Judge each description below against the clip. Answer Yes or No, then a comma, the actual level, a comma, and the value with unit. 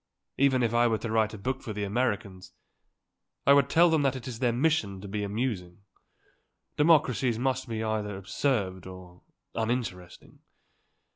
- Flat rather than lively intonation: No, average, 4.6 semitones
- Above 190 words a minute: No, average, 155 wpm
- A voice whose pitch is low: Yes, low, 115 Hz